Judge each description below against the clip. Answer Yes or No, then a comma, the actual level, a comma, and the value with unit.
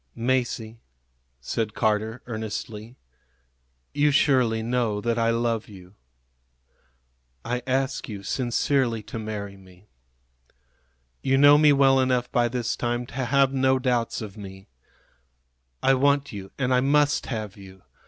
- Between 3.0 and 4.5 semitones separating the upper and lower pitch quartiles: Yes, average, 3.6 semitones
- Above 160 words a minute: No, slow, 135 wpm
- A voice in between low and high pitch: No, low, 120 Hz